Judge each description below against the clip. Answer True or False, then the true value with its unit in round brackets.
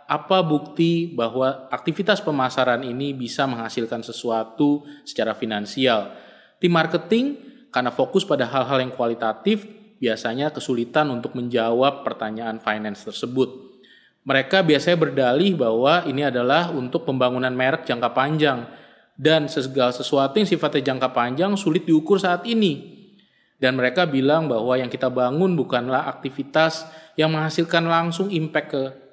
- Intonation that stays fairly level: False (4.7 semitones)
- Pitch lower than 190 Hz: True (140 Hz)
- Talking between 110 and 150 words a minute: True (130 wpm)